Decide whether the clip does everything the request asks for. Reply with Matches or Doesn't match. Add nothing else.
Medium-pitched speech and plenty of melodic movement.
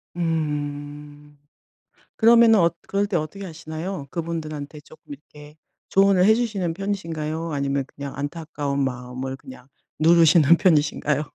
Doesn't match